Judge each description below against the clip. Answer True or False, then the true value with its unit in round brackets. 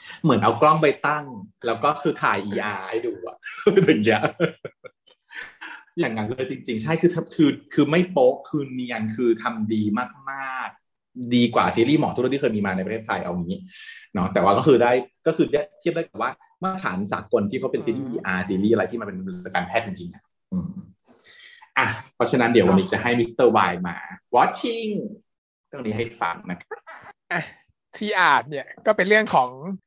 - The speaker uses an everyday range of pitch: False (8.7 semitones)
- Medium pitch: True (160 Hz)